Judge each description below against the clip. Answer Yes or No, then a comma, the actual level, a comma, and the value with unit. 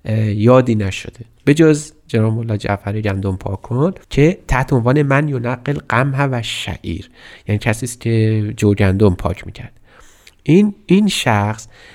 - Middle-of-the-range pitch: No, low, 115 Hz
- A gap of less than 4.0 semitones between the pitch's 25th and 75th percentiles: No, average, 4.8 semitones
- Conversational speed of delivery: Yes, average, 145 wpm